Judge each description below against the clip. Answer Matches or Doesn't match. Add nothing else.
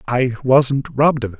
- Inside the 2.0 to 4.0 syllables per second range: Doesn't match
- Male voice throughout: Matches